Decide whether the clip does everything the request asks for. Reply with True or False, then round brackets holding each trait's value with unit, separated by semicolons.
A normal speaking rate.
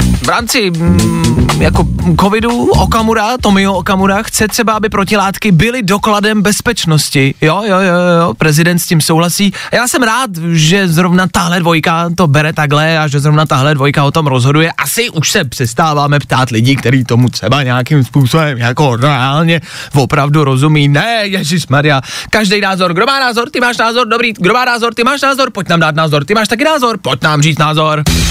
False (180 wpm)